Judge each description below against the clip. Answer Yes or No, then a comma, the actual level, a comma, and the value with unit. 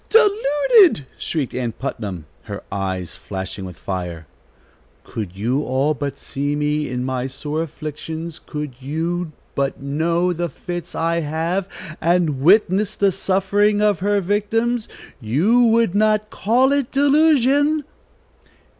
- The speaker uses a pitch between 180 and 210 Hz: No, medium, 165 Hz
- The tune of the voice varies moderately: No, wide, 7.7 semitones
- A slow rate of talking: Yes, slow, 130 wpm